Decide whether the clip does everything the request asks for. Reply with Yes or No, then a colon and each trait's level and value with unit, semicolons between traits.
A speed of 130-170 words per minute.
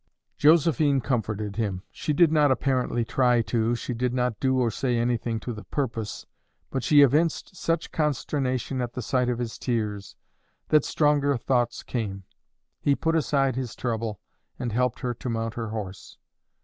Yes: average, 165 wpm